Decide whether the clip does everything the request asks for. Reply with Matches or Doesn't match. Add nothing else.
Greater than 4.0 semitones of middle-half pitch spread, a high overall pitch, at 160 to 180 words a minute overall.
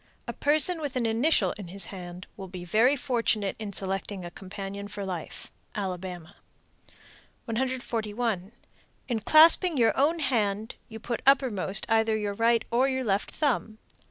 Doesn't match